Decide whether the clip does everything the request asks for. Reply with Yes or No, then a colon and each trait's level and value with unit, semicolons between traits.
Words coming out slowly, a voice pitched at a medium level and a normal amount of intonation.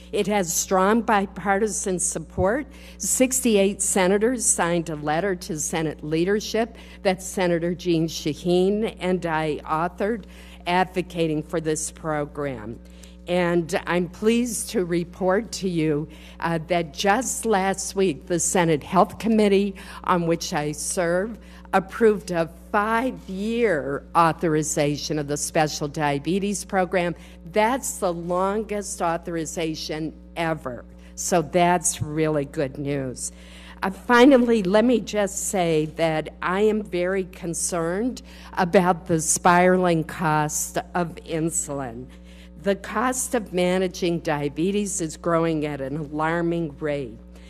Yes: slow, 115 wpm; medium, 175 Hz; average, 3.9 semitones